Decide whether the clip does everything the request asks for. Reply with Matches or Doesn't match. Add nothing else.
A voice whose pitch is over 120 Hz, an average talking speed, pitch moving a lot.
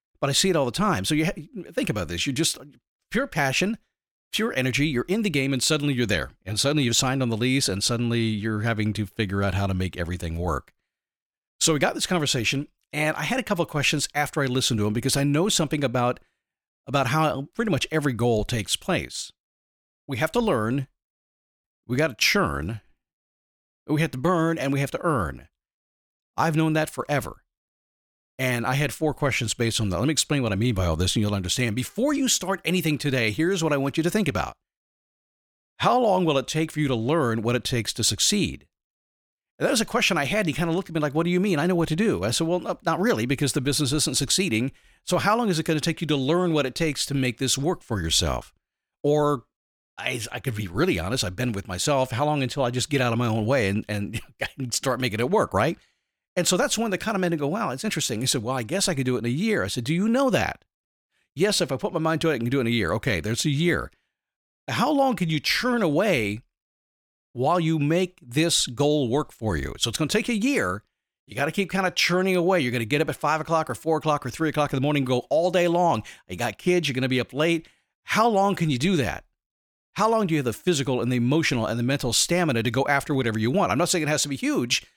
Doesn't match